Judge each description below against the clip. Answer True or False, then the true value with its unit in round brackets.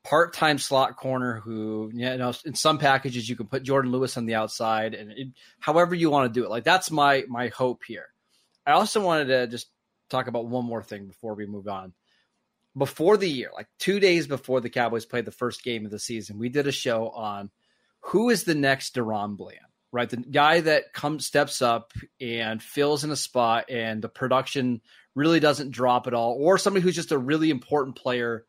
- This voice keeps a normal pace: False (210 wpm)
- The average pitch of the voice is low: True (125 Hz)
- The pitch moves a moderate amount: True (3.7 semitones)